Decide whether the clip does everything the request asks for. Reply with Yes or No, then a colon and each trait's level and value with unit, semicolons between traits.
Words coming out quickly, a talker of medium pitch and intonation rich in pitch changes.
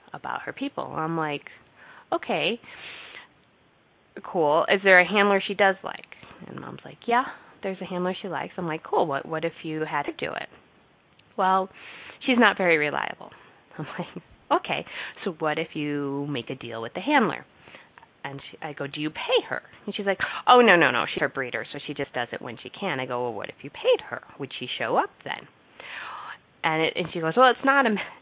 Yes: fast, 215 wpm; medium, 170 Hz; wide, 5.9 semitones